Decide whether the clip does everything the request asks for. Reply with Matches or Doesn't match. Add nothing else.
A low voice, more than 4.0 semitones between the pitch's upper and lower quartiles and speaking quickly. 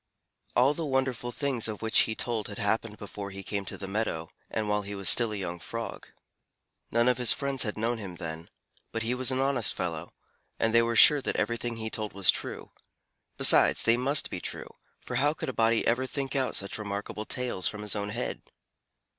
Doesn't match